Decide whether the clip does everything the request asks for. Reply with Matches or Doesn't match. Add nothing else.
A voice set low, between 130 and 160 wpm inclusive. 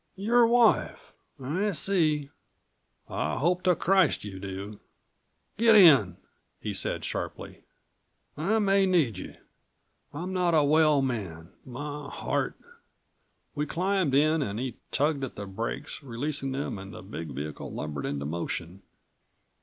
Doesn't match